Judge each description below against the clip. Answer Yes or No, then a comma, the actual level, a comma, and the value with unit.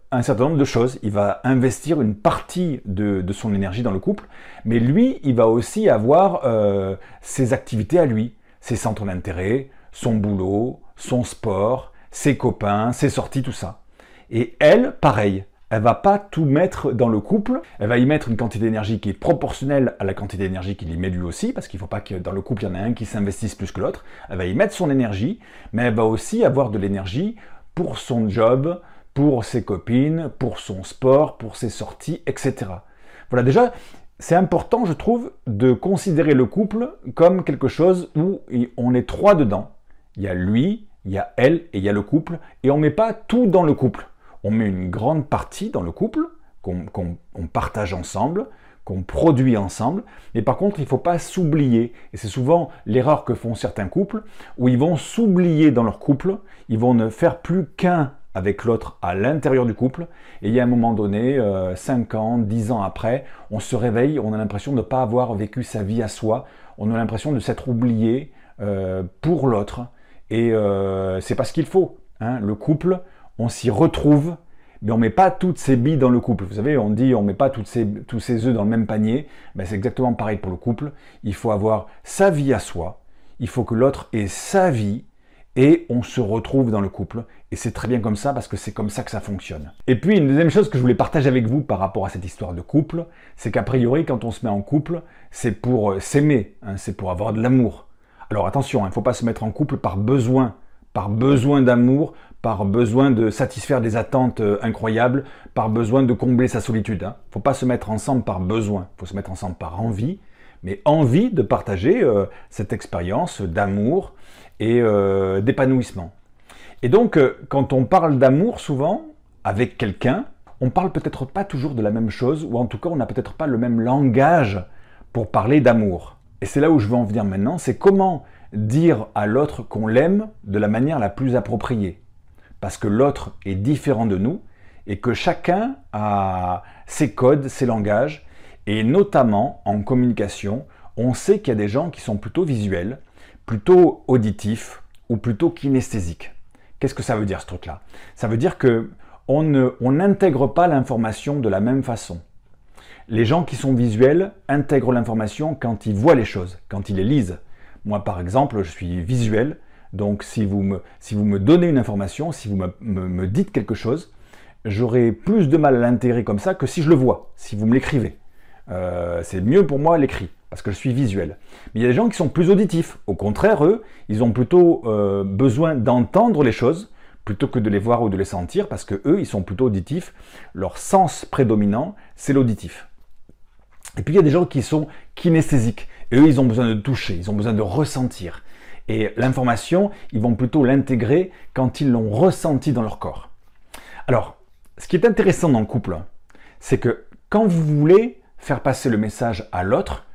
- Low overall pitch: Yes, low, 120 Hz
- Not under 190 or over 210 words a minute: Yes, average, 205 wpm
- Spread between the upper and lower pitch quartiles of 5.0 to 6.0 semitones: Yes, average, 5.3 semitones